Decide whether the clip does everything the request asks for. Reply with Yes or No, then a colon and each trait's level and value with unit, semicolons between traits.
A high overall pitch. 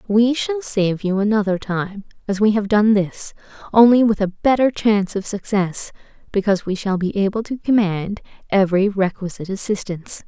Yes: high, 205 Hz